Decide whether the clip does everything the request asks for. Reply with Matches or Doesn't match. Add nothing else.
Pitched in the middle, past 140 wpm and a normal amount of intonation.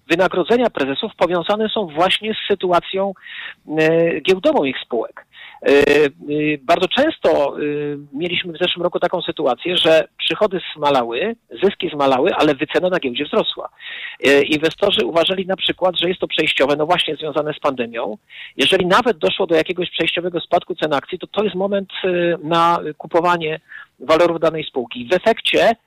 Matches